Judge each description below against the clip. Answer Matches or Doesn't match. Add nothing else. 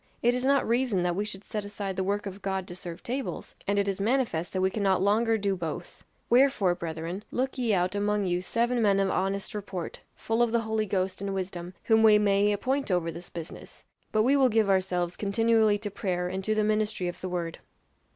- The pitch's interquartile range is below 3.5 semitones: Matches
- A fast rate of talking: Matches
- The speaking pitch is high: Matches